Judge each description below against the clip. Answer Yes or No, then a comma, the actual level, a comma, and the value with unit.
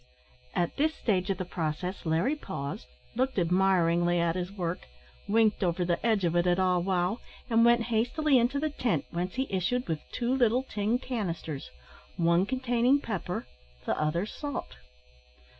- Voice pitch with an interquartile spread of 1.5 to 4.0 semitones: No, wide, 5.6 semitones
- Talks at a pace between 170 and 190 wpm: No, average, 160 wpm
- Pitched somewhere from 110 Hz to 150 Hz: No, high, 190 Hz